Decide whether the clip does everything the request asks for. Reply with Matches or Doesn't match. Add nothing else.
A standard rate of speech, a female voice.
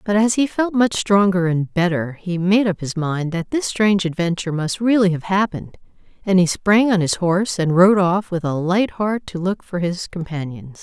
Doesn't match